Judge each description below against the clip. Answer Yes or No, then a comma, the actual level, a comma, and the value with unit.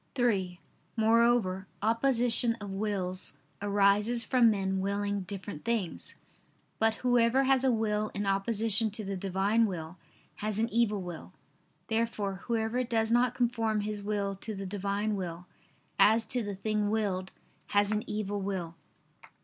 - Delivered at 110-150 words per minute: Yes, average, 140 wpm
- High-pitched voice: Yes, high, 210 Hz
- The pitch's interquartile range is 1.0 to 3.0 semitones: Yes, narrow, 2.6 semitones